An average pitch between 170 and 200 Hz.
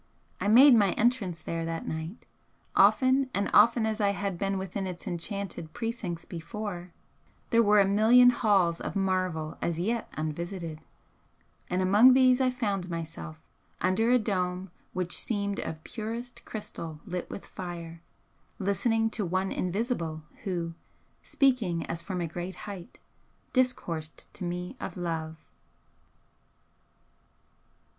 Yes: high, 190 Hz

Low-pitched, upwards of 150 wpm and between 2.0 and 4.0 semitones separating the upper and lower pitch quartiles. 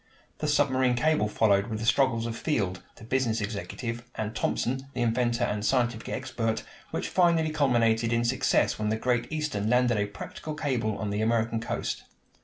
Yes: low, 120 Hz; average, 175 wpm; average, 2.9 semitones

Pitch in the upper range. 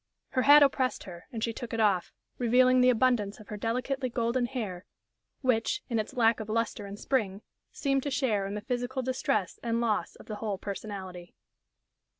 Yes: high, 230 Hz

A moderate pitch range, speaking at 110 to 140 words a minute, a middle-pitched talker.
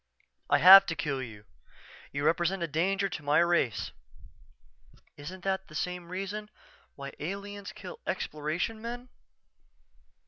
Yes: average, 4.3 semitones; slow, 135 wpm; medium, 175 Hz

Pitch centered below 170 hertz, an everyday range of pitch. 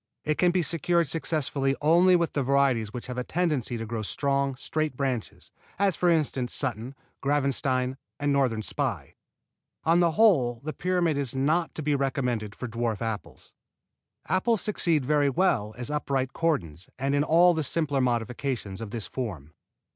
Yes: medium, 140 Hz; average, 4.6 semitones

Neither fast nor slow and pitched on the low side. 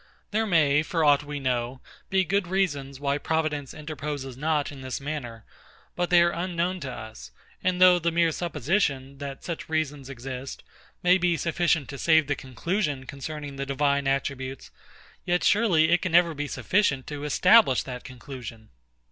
No: average, 165 wpm; medium, 150 Hz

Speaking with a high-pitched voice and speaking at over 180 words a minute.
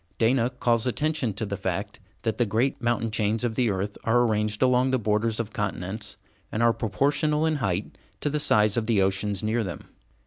No: low, 115 Hz; average, 200 wpm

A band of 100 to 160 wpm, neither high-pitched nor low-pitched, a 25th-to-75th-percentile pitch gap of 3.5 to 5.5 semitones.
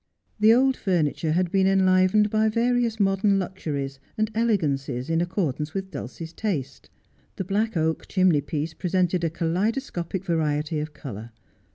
Yes: average, 140 wpm; medium, 180 Hz; average, 4.7 semitones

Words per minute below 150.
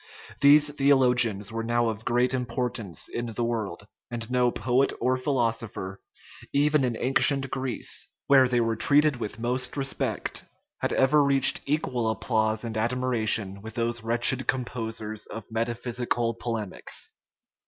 Yes: slow, 135 wpm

